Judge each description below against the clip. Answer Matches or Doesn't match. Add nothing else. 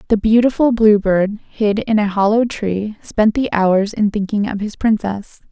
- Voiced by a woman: Matches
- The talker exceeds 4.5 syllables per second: Doesn't match